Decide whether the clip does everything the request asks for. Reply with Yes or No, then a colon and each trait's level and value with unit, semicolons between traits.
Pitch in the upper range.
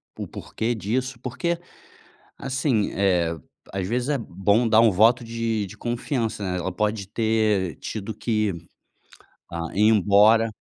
No: low, 110 Hz